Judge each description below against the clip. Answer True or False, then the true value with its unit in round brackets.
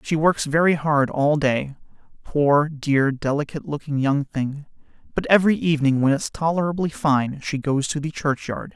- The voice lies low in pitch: False (150 Hz)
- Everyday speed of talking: True (160 wpm)